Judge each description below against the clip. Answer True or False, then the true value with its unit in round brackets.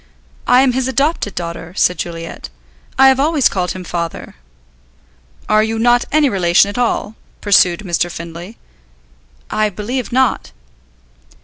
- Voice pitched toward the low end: False (210 Hz)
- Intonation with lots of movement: True (6.4 semitones)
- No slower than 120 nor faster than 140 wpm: True (135 wpm)